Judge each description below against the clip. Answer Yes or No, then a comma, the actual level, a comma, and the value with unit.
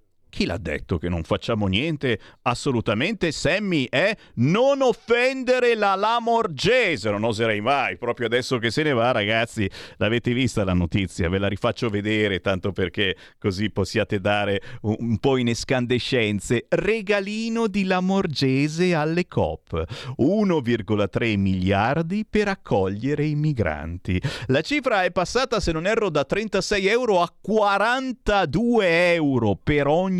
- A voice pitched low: Yes, low, 130 Hz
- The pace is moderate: Yes, average, 135 wpm